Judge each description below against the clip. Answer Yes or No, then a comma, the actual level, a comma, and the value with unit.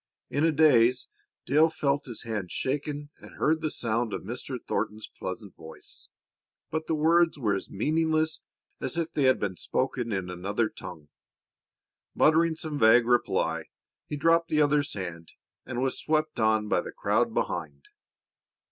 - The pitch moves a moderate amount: No, wide, 6.7 semitones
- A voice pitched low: Yes, low, 130 Hz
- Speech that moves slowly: No, average, 155 wpm